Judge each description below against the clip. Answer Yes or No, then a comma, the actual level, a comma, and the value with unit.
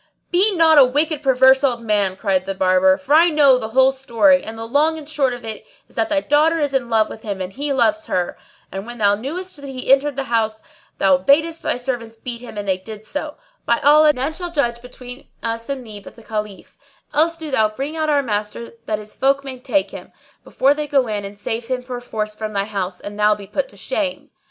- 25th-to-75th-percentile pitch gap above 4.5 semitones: Yes, average, 5.1 semitones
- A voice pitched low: No, very high, 250 Hz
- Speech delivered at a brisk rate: Yes, fast, 240 wpm